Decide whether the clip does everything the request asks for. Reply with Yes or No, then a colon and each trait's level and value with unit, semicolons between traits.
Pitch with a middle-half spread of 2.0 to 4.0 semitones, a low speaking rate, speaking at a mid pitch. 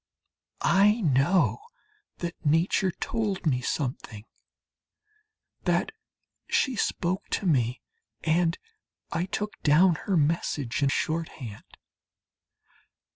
No: average, 4.9 semitones; slow, 95 wpm; medium, 165 Hz